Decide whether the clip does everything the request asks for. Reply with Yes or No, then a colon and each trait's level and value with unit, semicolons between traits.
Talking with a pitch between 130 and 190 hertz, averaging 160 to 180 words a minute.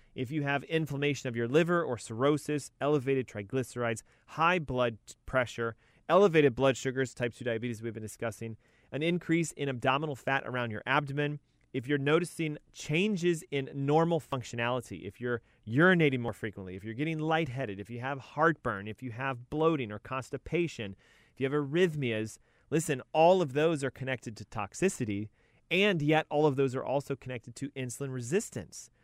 Yes: low, 135 Hz; average, 165 wpm